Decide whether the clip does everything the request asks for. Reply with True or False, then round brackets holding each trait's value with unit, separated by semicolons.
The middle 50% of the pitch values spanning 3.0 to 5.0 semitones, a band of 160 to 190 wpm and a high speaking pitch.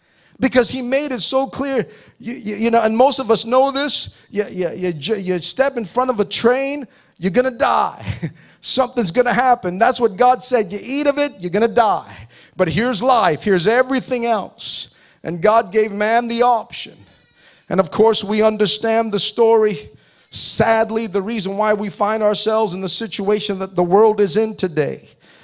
True (3.4 semitones; 185 wpm; 225 Hz)